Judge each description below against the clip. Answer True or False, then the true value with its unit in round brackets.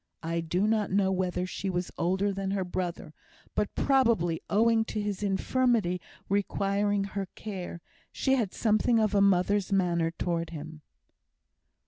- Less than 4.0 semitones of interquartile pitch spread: True (2.7 semitones)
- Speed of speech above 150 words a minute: False (145 wpm)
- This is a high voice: True (195 Hz)